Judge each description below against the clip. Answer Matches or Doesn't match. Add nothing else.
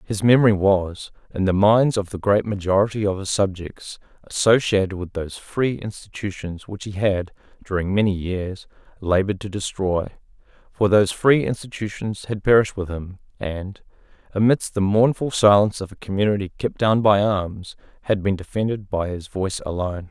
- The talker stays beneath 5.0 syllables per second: Doesn't match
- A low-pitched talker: Matches